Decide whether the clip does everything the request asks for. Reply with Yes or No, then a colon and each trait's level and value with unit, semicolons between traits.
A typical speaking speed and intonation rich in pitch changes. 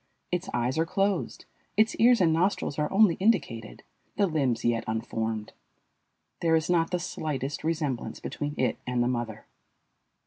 Yes: average, 150 wpm; wide, 6.7 semitones